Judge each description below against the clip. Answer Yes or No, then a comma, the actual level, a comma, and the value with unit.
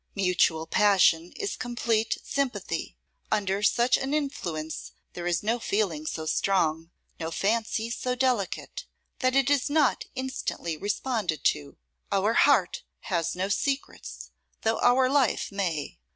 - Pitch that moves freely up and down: Yes, wide, 6.7 semitones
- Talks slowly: Yes, slow, 130 wpm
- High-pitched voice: Yes, high, 210 Hz